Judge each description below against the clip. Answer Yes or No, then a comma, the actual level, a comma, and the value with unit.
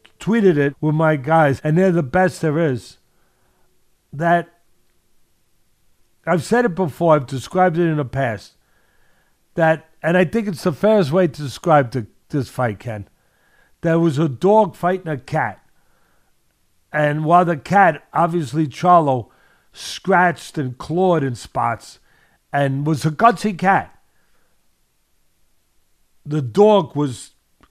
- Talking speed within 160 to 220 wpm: No, slow, 135 wpm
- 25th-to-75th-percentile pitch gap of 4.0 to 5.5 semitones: Yes, average, 5.0 semitones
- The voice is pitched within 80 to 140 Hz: No, medium, 160 Hz